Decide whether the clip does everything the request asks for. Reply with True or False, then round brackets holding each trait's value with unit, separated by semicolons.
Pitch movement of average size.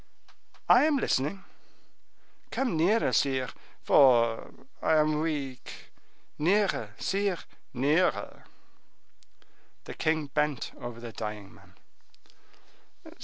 False (6.3 semitones)